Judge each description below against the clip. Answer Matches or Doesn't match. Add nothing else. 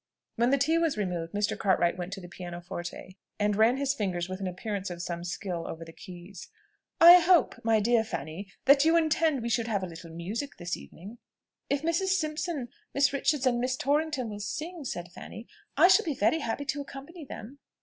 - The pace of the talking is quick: Matches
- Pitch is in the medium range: Doesn't match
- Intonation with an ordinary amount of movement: Doesn't match